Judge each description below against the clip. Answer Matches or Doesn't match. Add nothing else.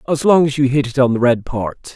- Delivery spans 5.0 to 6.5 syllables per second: Matches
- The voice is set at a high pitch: Doesn't match